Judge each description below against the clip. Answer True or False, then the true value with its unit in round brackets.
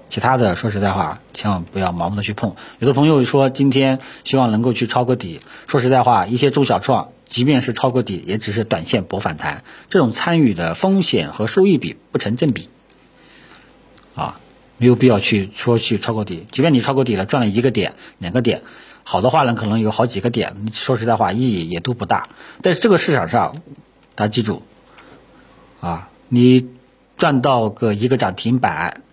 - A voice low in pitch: True (120 Hz)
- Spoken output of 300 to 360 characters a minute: False (280 characters per minute)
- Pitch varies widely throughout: False (3.3 semitones)